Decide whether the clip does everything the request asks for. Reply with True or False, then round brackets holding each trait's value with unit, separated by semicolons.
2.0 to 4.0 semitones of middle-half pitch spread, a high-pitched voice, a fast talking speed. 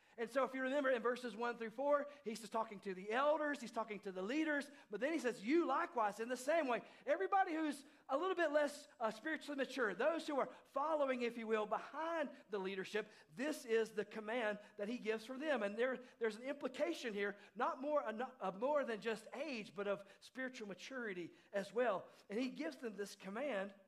False (5.1 semitones; 245 Hz; 210 wpm)